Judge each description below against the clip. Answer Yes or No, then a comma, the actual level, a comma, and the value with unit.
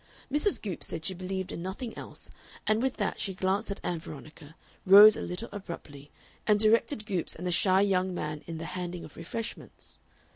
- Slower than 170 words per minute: No, average, 190 wpm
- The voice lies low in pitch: No, medium, 185 Hz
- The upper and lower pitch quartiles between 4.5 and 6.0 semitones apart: No, average, 3.8 semitones